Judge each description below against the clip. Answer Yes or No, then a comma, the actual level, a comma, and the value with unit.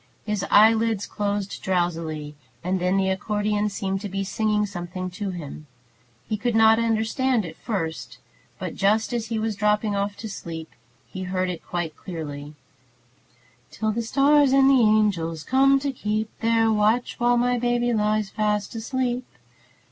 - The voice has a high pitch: Yes, high, 210 Hz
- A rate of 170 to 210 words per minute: No, average, 155 wpm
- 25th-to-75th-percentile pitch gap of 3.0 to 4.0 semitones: Yes, average, 3.3 semitones